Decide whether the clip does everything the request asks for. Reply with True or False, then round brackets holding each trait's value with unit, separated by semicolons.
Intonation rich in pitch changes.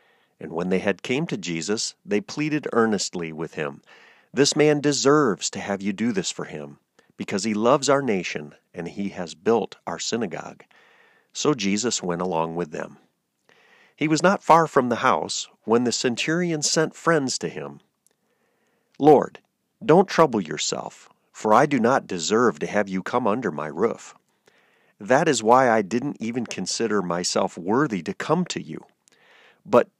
True (7.3 semitones)